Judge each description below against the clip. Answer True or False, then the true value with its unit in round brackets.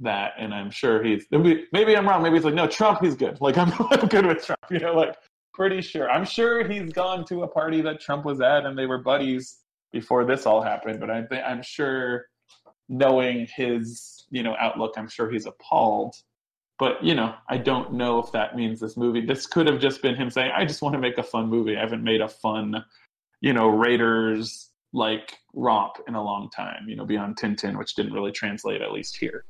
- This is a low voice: True (130 Hz)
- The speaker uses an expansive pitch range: True (6.4 semitones)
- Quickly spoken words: True (220 wpm)